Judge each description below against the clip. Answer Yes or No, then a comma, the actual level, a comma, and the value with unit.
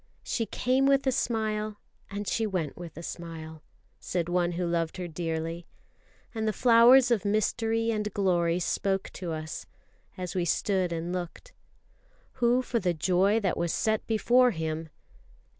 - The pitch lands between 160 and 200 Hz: Yes, high, 190 Hz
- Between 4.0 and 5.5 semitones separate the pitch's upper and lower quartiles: Yes, average, 4.8 semitones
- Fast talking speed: No, average, 160 wpm